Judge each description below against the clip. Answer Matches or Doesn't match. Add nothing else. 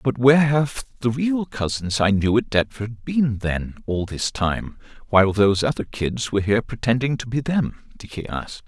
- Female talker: Doesn't match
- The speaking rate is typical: Matches